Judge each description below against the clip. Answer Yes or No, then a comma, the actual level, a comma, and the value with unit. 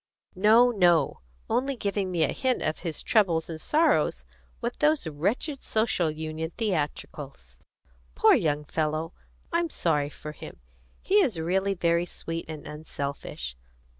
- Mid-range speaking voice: Yes, medium, 170 Hz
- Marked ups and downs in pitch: Yes, wide, 6.0 semitones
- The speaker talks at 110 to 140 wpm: Yes, slow, 135 wpm